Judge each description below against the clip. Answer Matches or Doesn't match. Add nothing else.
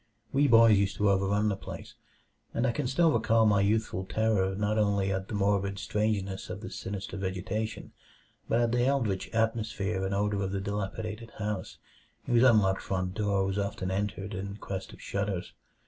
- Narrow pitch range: Matches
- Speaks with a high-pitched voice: Doesn't match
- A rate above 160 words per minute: Matches